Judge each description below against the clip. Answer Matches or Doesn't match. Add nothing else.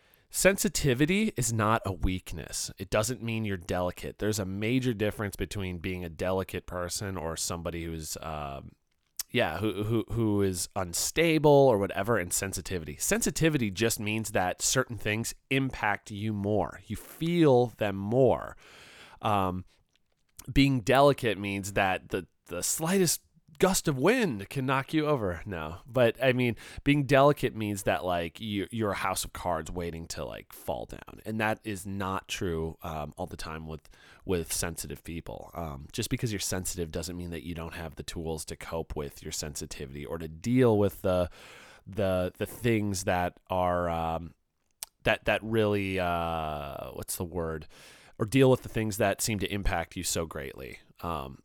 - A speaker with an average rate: Matches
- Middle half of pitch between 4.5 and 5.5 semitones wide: Matches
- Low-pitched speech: Matches